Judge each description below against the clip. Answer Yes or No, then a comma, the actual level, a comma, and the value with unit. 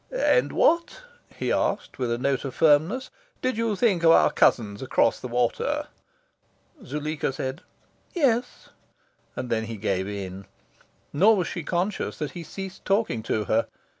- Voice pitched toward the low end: No, medium, 150 Hz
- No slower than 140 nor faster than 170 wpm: Yes, average, 155 wpm